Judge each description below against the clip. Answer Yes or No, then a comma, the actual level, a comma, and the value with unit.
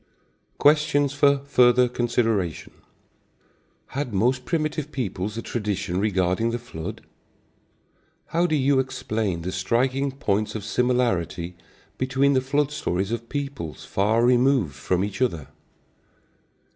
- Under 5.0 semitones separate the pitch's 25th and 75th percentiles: No, wide, 5.6 semitones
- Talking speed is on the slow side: Yes, slow, 120 wpm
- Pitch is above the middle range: No, low, 120 Hz